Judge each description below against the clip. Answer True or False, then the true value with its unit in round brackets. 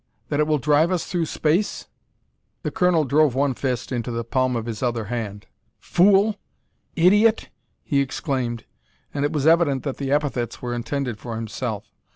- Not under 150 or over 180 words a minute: True (170 wpm)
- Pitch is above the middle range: False (140 Hz)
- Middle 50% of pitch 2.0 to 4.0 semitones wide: False (4.6 semitones)